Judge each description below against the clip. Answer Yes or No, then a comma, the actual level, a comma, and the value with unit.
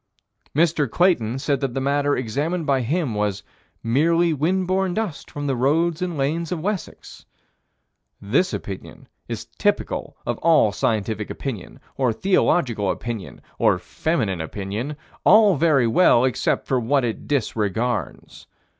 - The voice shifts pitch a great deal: Yes, wide, 6.6 semitones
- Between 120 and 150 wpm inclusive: Yes, slow, 135 wpm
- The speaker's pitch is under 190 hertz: Yes, medium, 140 Hz